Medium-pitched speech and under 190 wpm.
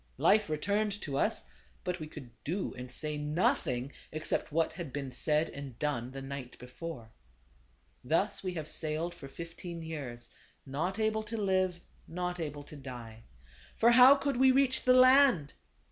Yes: medium, 160 Hz; average, 165 wpm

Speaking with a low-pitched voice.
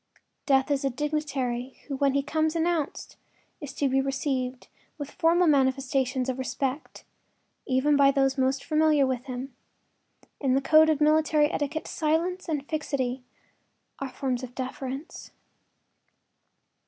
No: very high, 275 Hz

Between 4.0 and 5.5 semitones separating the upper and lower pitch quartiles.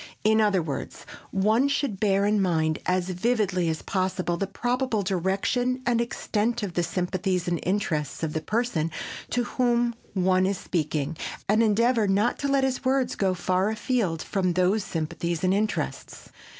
Yes: average, 4.7 semitones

